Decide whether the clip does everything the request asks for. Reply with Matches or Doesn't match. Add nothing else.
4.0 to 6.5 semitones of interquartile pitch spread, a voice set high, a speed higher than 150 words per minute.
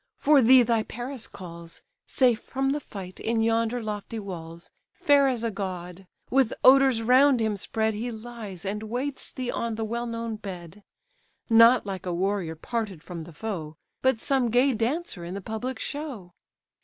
Matches